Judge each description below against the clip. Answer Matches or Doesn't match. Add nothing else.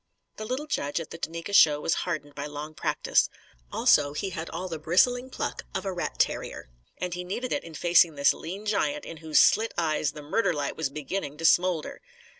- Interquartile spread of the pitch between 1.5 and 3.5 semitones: Doesn't match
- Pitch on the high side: Doesn't match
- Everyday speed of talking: Doesn't match